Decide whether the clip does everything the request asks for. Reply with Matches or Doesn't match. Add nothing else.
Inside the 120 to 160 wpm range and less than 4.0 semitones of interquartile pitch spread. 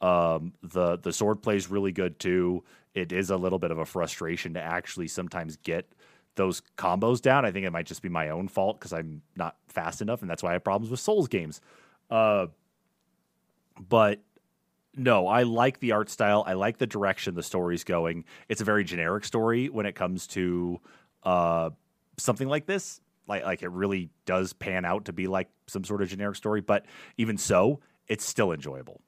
Doesn't match